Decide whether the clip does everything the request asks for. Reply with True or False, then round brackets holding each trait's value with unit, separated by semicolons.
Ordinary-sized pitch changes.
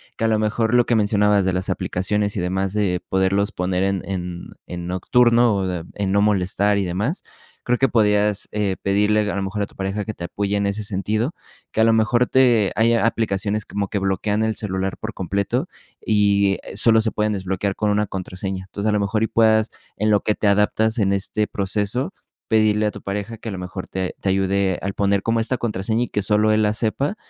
False (2.1 semitones)